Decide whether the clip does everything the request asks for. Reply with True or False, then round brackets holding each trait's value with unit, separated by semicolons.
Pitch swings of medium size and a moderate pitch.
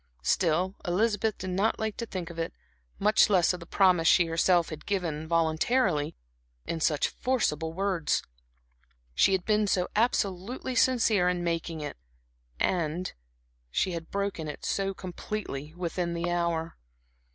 True (3.4 semitones; 180 Hz)